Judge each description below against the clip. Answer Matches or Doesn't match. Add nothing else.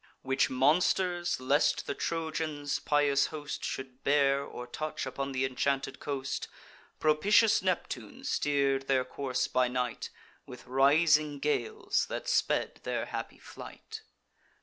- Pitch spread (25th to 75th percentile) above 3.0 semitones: Doesn't match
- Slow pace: Matches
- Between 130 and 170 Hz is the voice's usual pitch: Matches